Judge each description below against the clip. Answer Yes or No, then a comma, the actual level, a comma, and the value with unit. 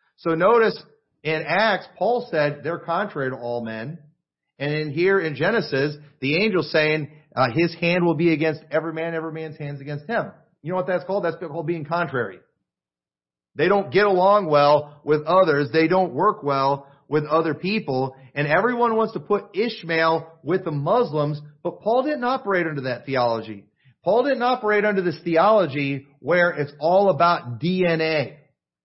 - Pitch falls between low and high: Yes, medium, 160 Hz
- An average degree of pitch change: Yes, average, 4.1 semitones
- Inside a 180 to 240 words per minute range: No, average, 170 wpm